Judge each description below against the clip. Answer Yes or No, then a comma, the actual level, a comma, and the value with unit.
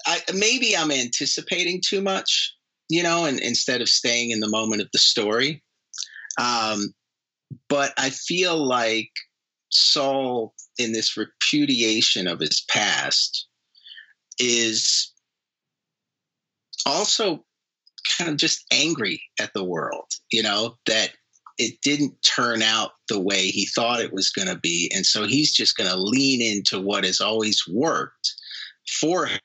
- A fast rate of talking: No, average, 140 wpm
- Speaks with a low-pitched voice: Yes, low, 125 Hz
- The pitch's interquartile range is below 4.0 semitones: No, wide, 5.4 semitones